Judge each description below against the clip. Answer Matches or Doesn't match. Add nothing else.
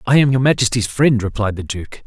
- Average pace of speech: Doesn't match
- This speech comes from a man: Matches